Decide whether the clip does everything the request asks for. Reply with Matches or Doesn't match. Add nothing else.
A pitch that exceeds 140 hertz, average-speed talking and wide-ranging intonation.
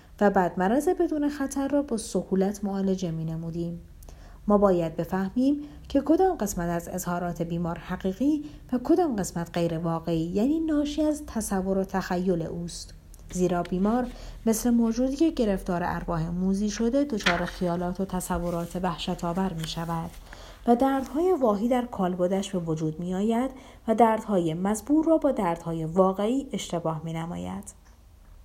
Matches